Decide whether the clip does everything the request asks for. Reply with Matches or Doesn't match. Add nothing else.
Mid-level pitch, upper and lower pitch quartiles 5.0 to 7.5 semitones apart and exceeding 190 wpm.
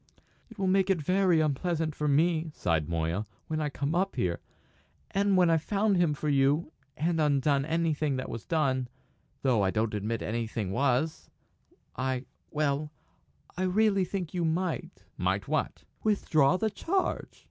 Doesn't match